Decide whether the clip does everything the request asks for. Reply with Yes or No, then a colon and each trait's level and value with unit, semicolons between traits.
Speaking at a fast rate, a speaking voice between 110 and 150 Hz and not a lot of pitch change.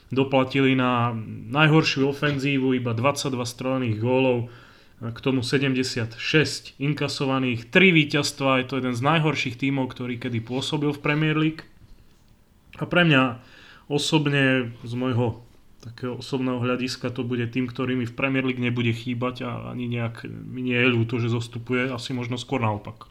No: average, 150 wpm; low, 130 Hz; narrow, 2.2 semitones